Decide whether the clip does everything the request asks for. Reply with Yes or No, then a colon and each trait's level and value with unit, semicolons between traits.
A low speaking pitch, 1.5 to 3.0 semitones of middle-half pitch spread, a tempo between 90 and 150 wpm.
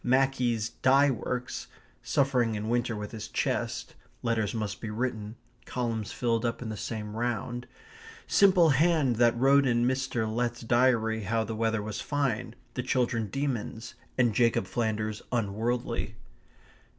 Yes: low, 120 Hz; narrow, 2.4 semitones; average, 140 wpm